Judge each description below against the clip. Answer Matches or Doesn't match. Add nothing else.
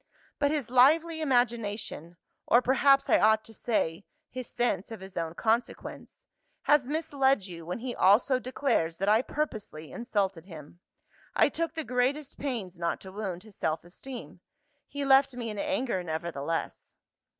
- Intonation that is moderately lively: Doesn't match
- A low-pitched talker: Doesn't match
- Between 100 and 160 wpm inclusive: Matches